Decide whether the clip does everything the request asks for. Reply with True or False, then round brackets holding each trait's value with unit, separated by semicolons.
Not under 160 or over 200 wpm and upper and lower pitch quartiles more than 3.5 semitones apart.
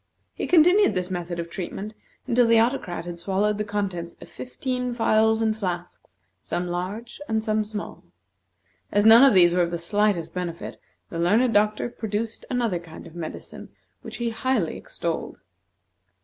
True (165 wpm; 4.5 semitones)